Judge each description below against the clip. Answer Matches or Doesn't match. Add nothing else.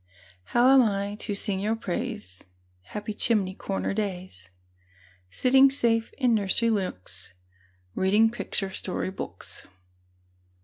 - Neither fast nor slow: Doesn't match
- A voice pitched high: Matches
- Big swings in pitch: Doesn't match